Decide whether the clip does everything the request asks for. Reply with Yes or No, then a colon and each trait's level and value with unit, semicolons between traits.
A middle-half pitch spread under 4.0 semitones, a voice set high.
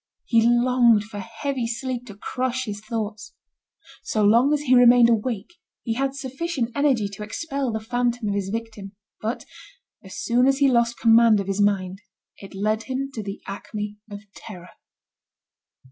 Yes: average, 3.5 semitones; high, 230 Hz